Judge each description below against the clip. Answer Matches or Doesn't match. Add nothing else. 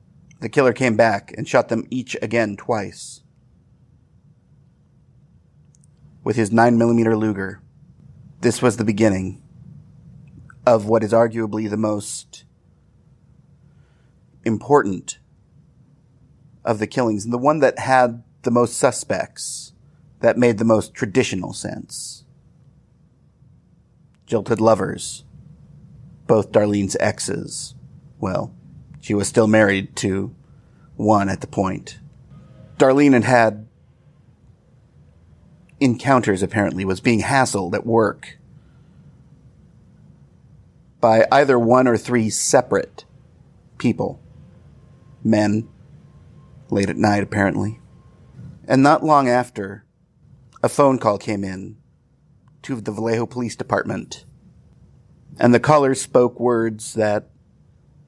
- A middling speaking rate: Doesn't match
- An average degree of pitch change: Matches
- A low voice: Matches